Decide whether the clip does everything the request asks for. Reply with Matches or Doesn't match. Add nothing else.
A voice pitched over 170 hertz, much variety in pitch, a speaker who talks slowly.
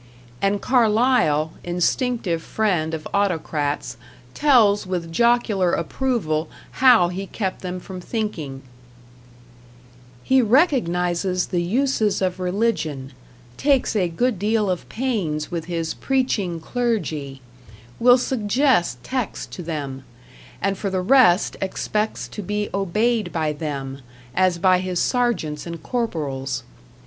Matches